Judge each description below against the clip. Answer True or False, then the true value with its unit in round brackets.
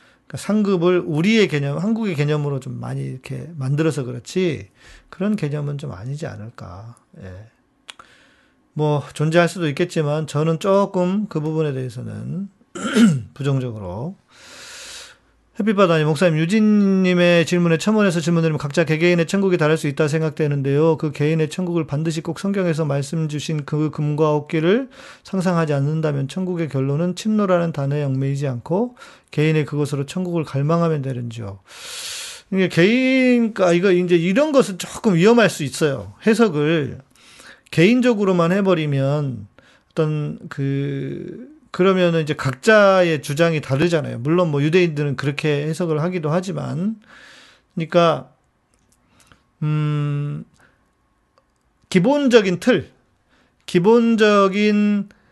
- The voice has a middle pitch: True (160 Hz)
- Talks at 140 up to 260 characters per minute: False (295 characters per minute)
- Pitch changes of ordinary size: True (4.5 semitones)